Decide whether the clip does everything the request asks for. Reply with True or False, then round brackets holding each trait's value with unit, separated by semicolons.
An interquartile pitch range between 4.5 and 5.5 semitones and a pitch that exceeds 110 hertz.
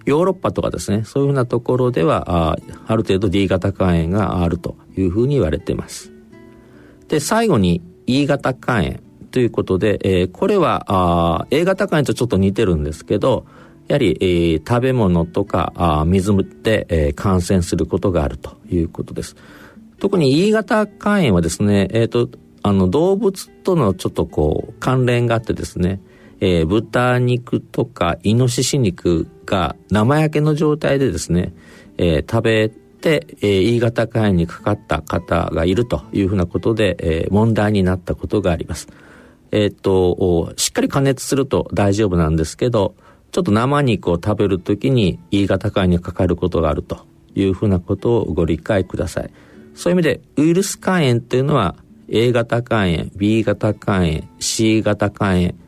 False (5.2 semitones; 100 Hz)